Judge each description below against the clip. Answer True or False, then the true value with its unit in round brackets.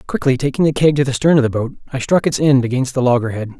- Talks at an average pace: False (285 wpm)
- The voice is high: False (130 Hz)